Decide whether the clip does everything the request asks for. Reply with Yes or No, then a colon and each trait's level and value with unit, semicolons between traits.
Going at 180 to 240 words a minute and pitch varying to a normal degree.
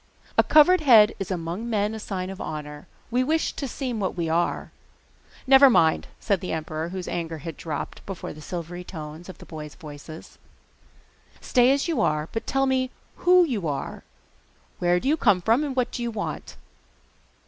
No: average, 185 wpm; wide, 7.7 semitones